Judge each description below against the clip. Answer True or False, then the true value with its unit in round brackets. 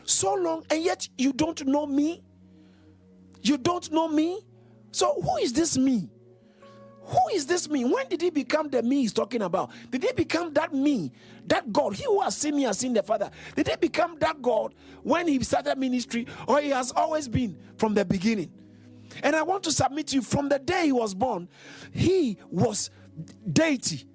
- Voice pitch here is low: False (280 Hz)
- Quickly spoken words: False (195 wpm)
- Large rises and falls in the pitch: True (7.4 semitones)